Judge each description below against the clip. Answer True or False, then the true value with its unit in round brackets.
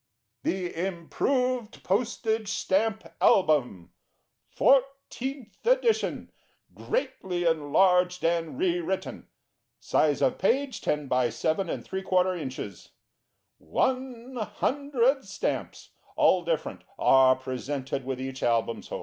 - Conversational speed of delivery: False (100 wpm)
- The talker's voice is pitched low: False (185 Hz)